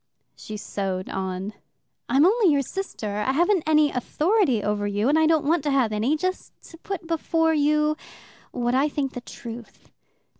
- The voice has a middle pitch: No, very high, 285 Hz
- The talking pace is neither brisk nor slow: Yes, average, 175 wpm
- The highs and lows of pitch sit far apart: Yes, wide, 6.8 semitones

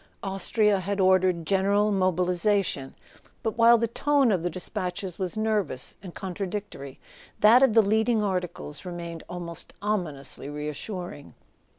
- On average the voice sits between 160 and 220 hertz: Yes, high, 190 Hz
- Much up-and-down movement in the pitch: No, average, 3.3 semitones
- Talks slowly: Yes, slow, 130 wpm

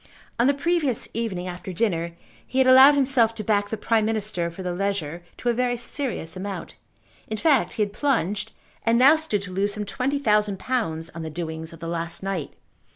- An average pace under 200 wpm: No, fast, 205 wpm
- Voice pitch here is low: No, high, 210 Hz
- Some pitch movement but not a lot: No, wide, 5.8 semitones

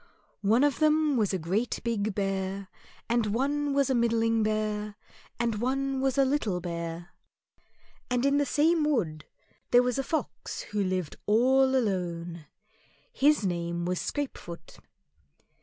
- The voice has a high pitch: Yes, high, 225 Hz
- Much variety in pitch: Yes, wide, 6.1 semitones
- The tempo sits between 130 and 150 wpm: Yes, average, 140 wpm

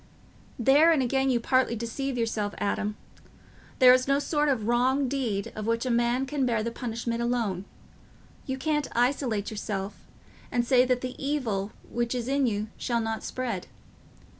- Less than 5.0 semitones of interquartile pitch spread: Yes, average, 3.0 semitones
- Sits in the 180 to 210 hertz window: No, high, 240 Hz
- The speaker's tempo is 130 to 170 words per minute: Yes, average, 165 wpm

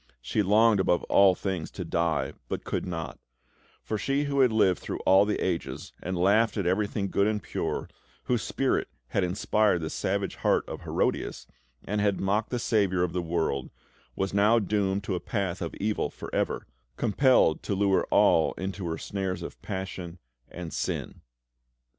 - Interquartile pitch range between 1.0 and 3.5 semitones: Yes, average, 2.8 semitones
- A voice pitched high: No, very low, 95 Hz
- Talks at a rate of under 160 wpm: No, average, 175 wpm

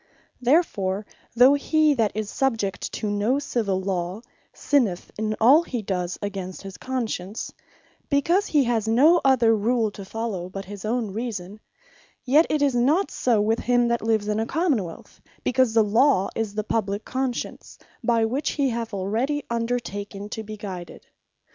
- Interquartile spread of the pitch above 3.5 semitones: Yes, average, 4.1 semitones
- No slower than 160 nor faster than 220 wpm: Yes, average, 165 wpm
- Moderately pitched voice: No, high, 225 Hz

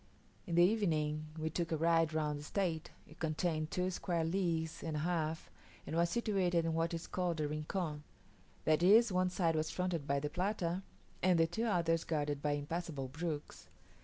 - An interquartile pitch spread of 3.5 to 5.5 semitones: No, narrow, 2.5 semitones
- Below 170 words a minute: No, average, 190 wpm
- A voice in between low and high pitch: Yes, medium, 165 Hz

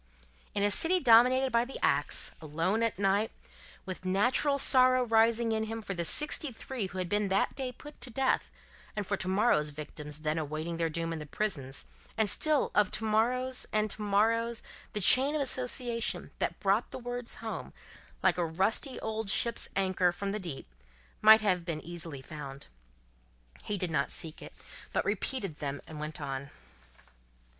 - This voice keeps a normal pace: Yes, average, 180 wpm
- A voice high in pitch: Yes, high, 205 Hz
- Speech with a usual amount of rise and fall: No, wide, 5.8 semitones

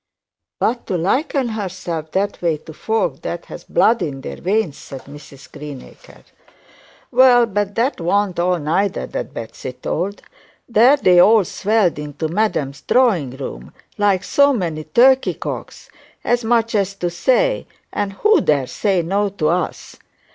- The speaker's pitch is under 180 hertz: No, high, 195 Hz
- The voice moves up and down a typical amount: No, wide, 6.1 semitones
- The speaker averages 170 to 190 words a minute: No, average, 145 wpm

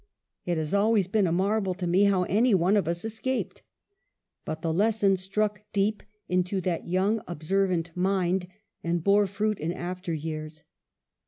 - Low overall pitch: No, high, 190 Hz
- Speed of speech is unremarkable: Yes, average, 160 wpm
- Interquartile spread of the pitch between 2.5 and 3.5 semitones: Yes, average, 2.9 semitones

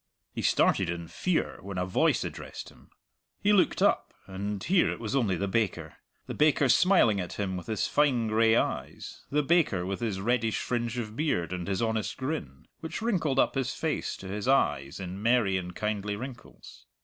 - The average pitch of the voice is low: Yes, low, 110 Hz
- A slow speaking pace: No, average, 190 wpm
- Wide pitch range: Yes, wide, 5.7 semitones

